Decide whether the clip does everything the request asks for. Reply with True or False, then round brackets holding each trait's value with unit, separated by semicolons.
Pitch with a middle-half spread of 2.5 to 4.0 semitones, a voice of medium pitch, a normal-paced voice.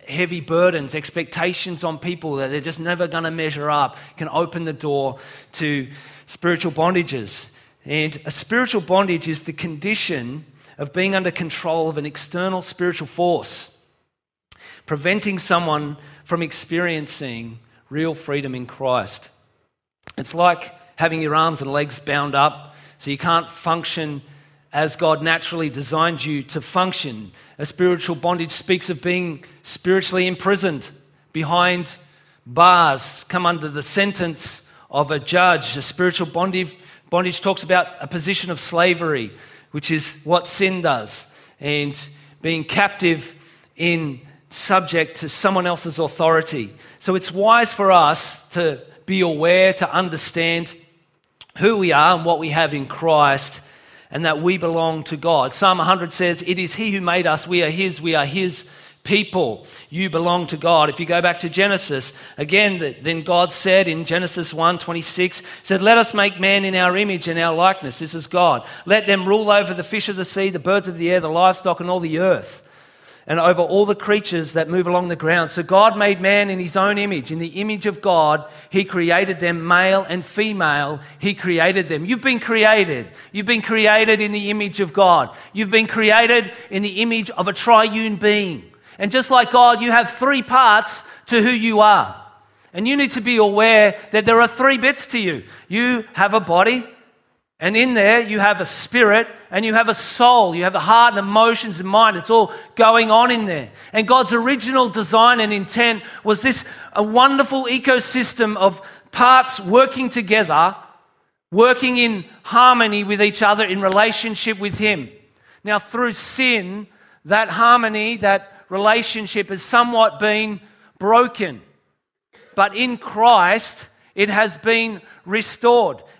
False (4.5 semitones; 180 Hz; 165 wpm)